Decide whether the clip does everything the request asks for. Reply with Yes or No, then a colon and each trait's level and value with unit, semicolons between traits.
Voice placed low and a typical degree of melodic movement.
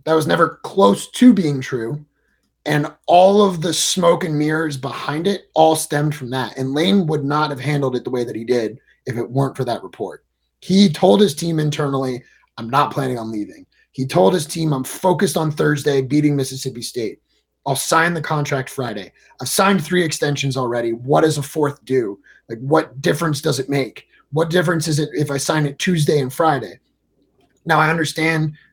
No: medium, 150 Hz; average, 3.4 semitones